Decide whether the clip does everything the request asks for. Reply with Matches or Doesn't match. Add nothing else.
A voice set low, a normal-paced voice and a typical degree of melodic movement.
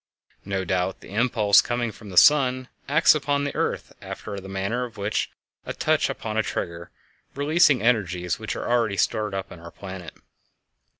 Matches